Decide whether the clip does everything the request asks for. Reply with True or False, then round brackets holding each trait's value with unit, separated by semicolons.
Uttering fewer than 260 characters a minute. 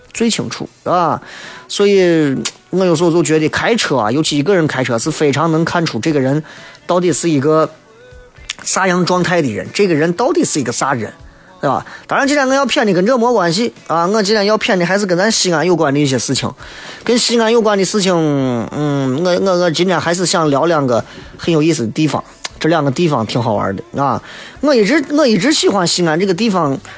False (310 characters per minute)